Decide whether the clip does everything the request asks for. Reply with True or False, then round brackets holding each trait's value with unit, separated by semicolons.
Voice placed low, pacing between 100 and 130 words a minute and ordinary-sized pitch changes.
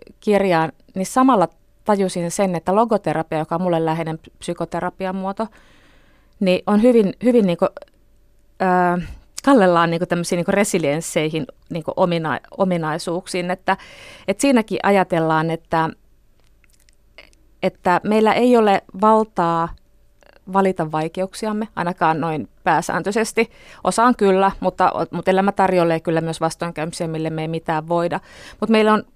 False (180 Hz; 115 wpm; 3.4 semitones)